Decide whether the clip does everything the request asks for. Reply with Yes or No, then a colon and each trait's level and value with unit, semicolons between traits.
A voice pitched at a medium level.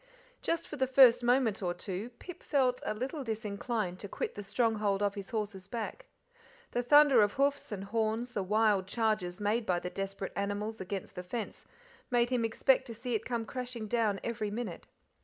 No: high, 220 Hz